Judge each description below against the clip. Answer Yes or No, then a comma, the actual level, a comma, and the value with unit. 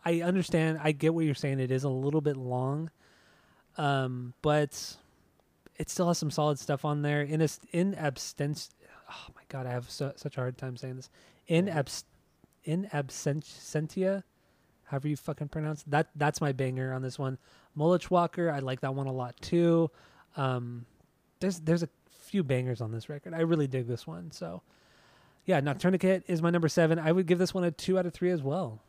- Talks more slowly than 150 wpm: No, average, 200 wpm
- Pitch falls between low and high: Yes, medium, 150 Hz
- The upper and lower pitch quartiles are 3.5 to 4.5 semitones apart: Yes, average, 4.2 semitones